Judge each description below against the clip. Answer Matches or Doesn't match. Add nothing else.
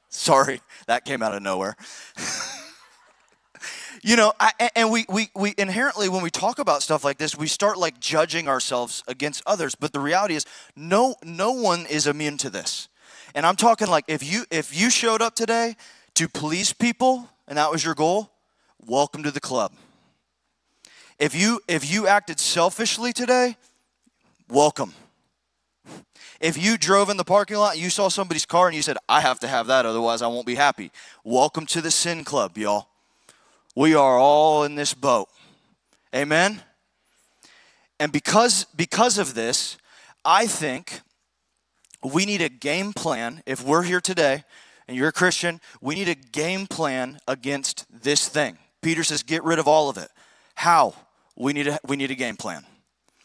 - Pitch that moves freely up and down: Matches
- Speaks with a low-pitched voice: Doesn't match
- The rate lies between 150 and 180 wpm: Matches